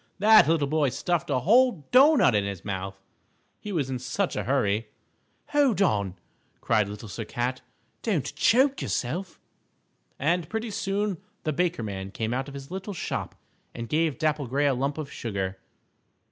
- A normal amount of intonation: No, wide, 8.7 semitones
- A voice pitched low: No, medium, 145 Hz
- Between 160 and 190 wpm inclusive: Yes, average, 165 wpm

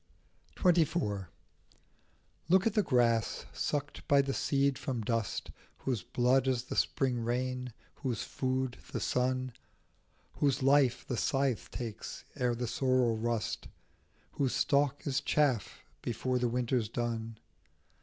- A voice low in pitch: Yes, low, 125 Hz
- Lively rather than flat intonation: No, narrow, 2.5 semitones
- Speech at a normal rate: No, slow, 130 wpm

